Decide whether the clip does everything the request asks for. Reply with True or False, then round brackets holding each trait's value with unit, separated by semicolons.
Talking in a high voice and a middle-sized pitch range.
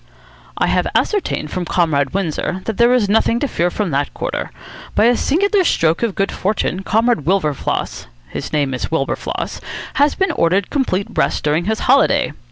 False (195 Hz; 6.6 semitones)